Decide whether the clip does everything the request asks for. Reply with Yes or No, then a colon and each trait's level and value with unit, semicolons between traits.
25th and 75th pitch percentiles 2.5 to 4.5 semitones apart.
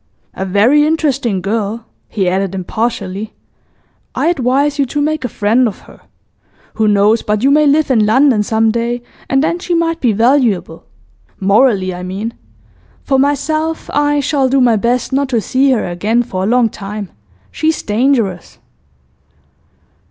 No: average, 5.3 semitones